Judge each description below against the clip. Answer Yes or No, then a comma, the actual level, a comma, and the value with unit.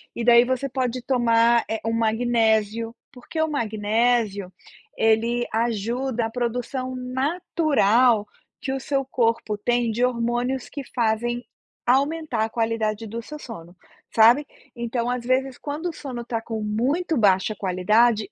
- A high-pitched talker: Yes, high, 235 Hz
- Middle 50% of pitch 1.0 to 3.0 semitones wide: Yes, narrow, 2.4 semitones